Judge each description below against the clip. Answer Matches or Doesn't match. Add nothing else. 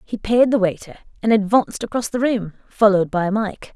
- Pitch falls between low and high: Doesn't match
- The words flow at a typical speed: Matches